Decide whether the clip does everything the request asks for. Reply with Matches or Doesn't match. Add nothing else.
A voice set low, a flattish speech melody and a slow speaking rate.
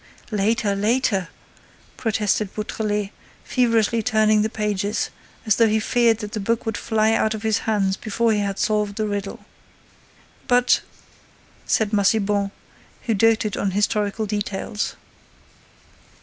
Doesn't match